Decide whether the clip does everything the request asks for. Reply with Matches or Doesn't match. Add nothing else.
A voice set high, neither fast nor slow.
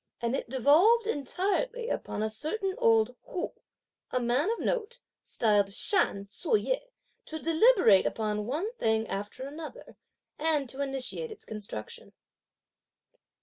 Doesn't match